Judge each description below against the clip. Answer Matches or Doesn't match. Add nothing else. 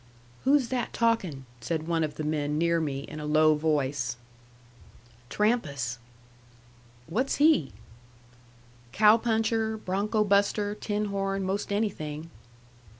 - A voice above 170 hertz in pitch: Matches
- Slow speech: Matches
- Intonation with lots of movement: Matches